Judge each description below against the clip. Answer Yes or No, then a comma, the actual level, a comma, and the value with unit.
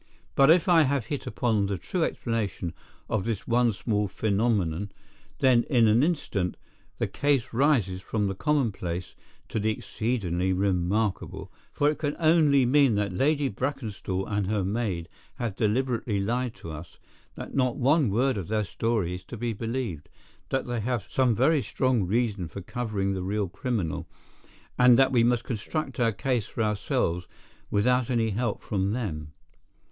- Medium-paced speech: Yes, average, 160 wpm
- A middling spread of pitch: Yes, average, 4.5 semitones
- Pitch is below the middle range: Yes, low, 115 Hz